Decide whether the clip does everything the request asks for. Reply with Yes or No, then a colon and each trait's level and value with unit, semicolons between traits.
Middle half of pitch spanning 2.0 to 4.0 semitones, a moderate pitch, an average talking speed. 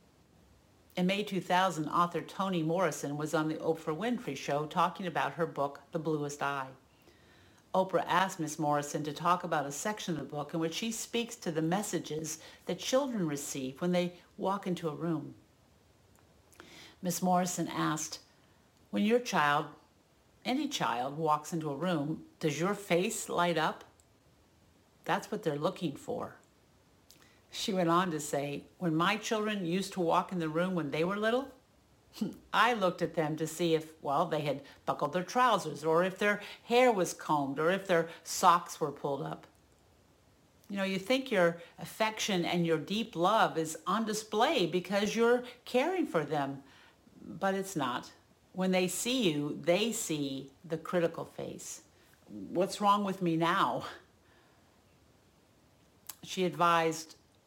Yes: average, 3.6 semitones; medium, 175 Hz; average, 155 wpm